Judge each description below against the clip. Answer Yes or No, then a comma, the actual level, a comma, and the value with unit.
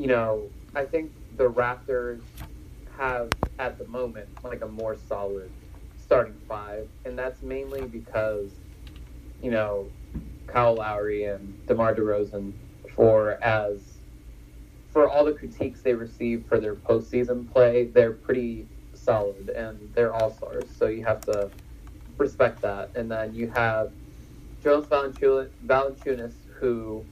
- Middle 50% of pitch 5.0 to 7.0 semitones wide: No, average, 3.5 semitones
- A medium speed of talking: No, slow, 130 wpm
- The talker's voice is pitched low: Yes, low, 110 Hz